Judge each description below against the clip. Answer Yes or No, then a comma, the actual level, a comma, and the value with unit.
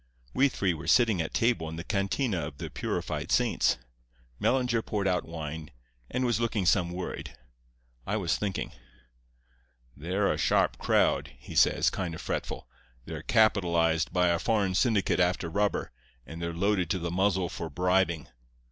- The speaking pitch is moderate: No, very low, 90 Hz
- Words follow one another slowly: No, average, 160 wpm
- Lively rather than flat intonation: No, average, 3.7 semitones